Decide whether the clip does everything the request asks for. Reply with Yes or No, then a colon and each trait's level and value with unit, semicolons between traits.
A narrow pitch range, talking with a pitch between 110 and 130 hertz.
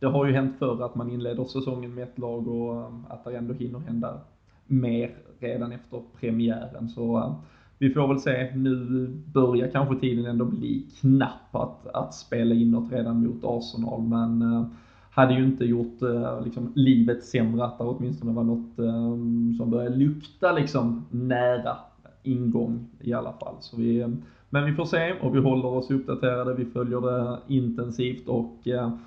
Yes: narrow, 1.7 semitones; low, 120 Hz